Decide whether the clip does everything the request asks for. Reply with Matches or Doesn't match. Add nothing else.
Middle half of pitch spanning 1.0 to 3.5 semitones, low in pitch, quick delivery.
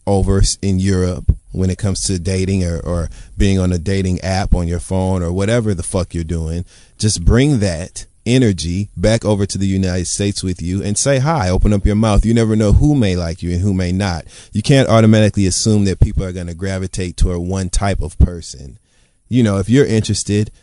Matches